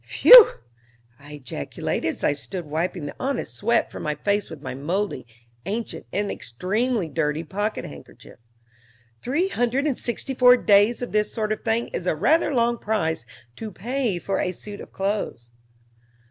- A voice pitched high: Yes, high, 205 Hz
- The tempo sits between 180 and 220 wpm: No, average, 165 wpm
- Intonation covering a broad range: Yes, wide, 6.8 semitones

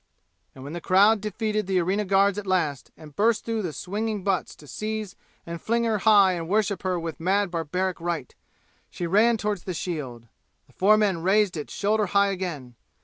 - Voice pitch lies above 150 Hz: Yes, high, 190 Hz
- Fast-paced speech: No, average, 195 wpm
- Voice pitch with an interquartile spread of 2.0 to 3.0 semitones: No, average, 3.8 semitones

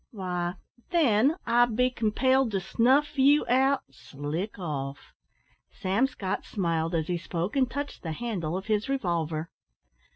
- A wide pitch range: Yes, wide, 7.2 semitones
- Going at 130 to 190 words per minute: Yes, average, 140 wpm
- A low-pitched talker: No, high, 205 Hz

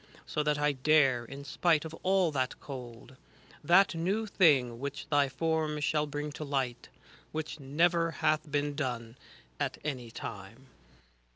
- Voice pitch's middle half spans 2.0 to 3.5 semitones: Yes, average, 3.2 semitones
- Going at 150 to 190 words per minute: Yes, average, 155 wpm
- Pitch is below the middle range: No, medium, 145 Hz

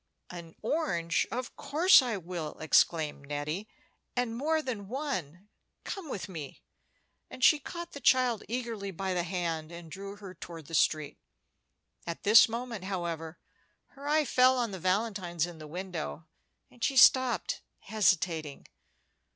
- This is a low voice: No, high, 195 Hz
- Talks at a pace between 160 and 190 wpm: No, average, 145 wpm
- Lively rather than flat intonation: Yes, wide, 7.0 semitones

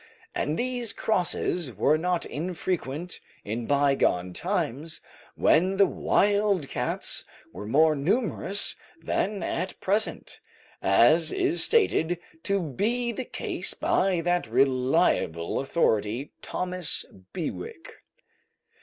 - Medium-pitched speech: Yes, medium, 170 Hz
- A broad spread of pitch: Yes, wide, 6.3 semitones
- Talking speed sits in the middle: No, slow, 100 wpm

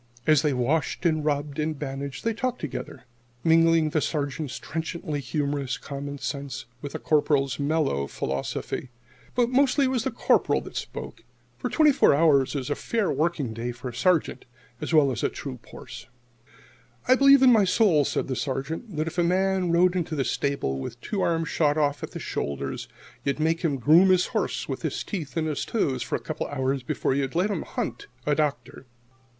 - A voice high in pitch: No, medium, 150 Hz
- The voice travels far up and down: No, average, 4.0 semitones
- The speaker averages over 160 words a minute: Yes, average, 200 wpm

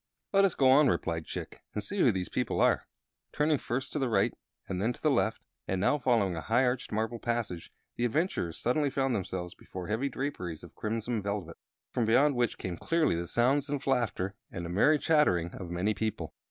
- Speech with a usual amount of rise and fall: No, wide, 6.5 semitones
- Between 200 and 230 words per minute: Yes, fast, 205 wpm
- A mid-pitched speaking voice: No, low, 115 Hz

